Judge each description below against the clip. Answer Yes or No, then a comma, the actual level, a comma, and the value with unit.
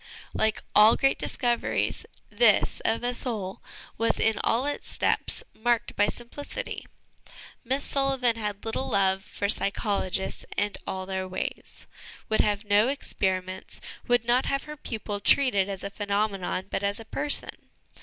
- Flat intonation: No, average, 3.5 semitones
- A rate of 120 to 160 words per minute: Yes, average, 145 wpm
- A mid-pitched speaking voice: No, high, 220 Hz